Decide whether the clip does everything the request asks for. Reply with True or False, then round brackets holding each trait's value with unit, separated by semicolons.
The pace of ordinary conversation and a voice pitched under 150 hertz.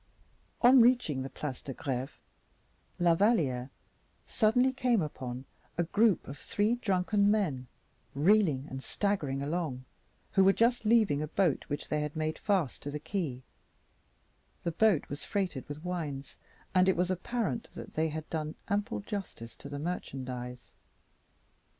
False (150 wpm; 165 Hz)